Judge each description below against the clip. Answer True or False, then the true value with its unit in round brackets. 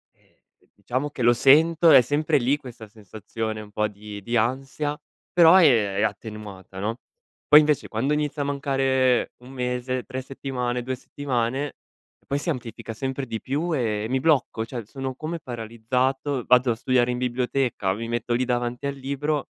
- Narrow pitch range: False (3.4 semitones)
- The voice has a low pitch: True (125 Hz)